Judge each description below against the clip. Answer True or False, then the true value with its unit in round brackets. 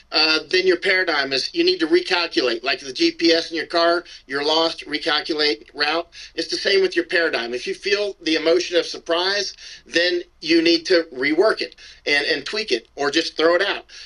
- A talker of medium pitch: True (175 Hz)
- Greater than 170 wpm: True (200 wpm)